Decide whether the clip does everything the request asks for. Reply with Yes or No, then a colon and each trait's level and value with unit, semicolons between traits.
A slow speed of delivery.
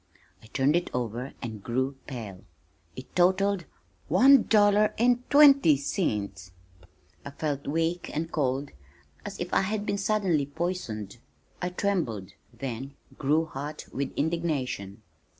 Yes: slow, 130 wpm